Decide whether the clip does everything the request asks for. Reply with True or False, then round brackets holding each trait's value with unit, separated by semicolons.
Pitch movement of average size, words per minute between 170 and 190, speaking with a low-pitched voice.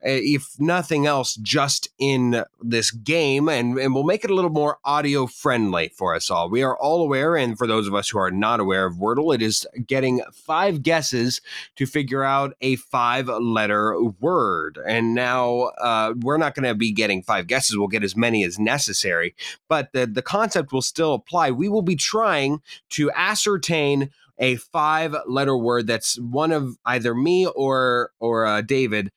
True (4.2 semitones; 185 wpm; 130 Hz)